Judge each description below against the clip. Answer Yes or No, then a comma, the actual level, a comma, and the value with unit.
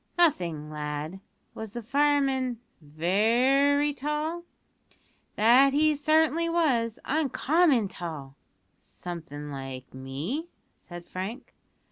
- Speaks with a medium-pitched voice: No, high, 235 Hz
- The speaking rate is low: Yes, slow, 90 wpm